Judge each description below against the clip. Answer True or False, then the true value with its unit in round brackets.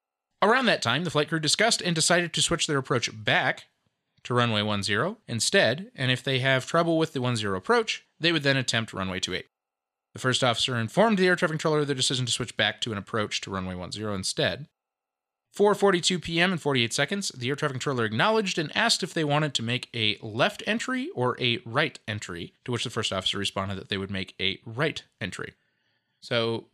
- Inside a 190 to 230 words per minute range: True (205 wpm)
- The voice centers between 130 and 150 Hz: True (135 Hz)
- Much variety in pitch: True (7.5 semitones)